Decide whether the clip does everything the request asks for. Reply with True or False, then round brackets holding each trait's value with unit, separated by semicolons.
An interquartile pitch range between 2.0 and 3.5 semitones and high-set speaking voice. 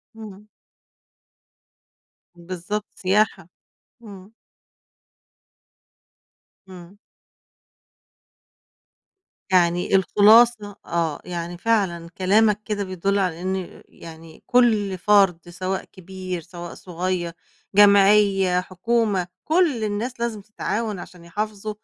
True (3.1 semitones; 195 Hz)